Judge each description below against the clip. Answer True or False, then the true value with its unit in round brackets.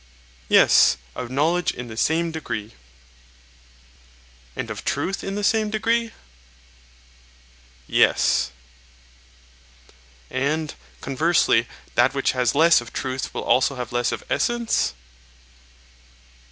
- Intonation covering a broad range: True (6.3 semitones)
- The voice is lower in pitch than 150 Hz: True (140 Hz)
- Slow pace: True (105 wpm)